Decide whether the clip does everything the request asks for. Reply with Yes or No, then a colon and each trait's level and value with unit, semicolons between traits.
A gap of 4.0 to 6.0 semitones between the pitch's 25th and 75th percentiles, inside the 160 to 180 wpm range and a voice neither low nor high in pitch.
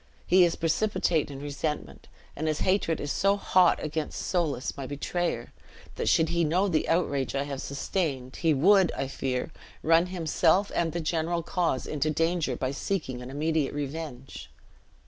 No: average, 3.6 semitones; average, 165 wpm; medium, 160 Hz